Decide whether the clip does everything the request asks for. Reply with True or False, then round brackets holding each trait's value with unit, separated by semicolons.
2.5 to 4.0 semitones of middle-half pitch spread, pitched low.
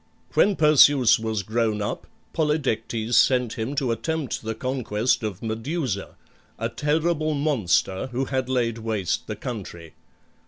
False (4.5 semitones; 120 Hz)